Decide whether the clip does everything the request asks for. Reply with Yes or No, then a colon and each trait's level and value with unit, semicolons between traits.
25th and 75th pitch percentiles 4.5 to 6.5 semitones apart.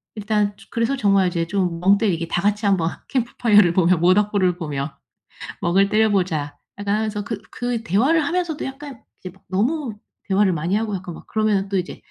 No: average, 3.6 semitones